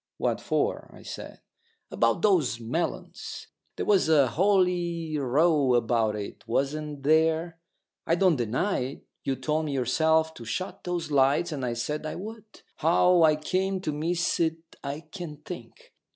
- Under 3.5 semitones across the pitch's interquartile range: No, average, 4.1 semitones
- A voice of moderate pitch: Yes, medium, 160 Hz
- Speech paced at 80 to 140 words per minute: No, average, 155 wpm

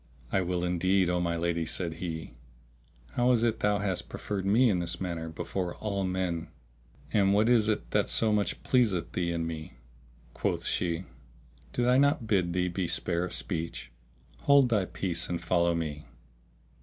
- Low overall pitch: Yes, very low, 90 Hz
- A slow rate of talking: No, average, 175 wpm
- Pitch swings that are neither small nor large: Yes, average, 3.5 semitones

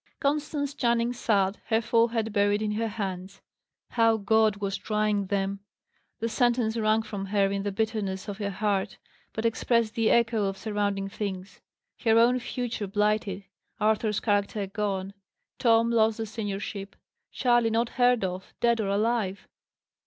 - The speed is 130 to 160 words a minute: Yes, average, 150 wpm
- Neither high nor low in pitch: No, high, 215 Hz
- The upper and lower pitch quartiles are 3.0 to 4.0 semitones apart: No, narrow, 2.4 semitones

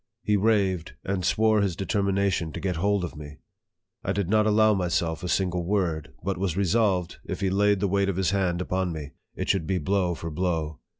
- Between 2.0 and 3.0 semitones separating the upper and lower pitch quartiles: Yes, narrow, 2.5 semitones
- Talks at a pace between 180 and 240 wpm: Yes, fast, 205 wpm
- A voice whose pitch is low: Yes, very low, 95 Hz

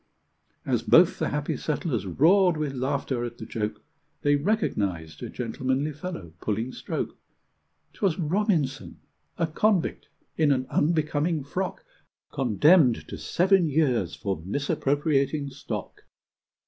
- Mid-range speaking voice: Yes, medium, 145 Hz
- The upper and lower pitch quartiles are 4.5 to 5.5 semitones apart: Yes, average, 5.1 semitones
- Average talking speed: No, slow, 120 wpm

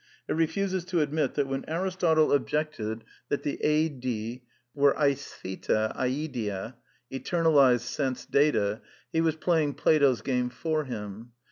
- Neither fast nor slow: No, slow, 125 wpm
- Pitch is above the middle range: No, medium, 140 Hz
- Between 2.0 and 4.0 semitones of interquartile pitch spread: No, average, 4.4 semitones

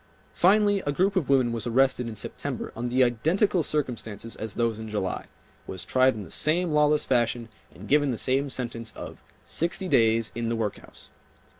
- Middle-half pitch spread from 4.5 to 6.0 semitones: Yes, average, 4.8 semitones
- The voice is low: Yes, low, 125 Hz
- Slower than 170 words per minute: No, average, 180 wpm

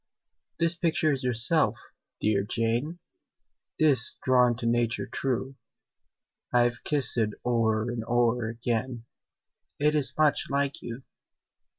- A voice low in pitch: Yes, low, 120 Hz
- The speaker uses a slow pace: Yes, slow, 115 wpm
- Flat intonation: No, average, 3.4 semitones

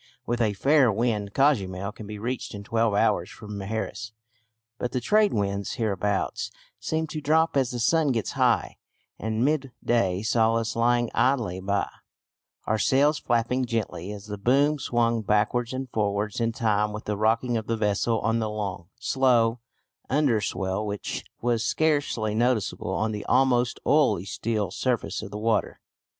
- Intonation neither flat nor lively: Yes, average, 3.1 semitones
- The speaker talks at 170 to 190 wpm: No, average, 160 wpm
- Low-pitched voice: Yes, low, 115 Hz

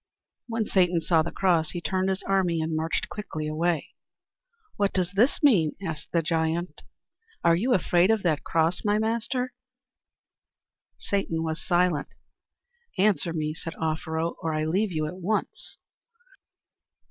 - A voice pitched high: No, medium, 175 Hz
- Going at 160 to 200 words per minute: No, average, 145 wpm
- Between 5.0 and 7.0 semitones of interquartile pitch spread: No, average, 3.4 semitones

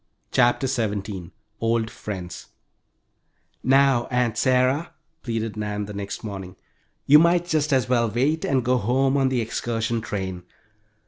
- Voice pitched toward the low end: Yes, low, 120 Hz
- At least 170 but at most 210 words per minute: No, slow, 135 wpm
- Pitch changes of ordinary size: Yes, average, 4.1 semitones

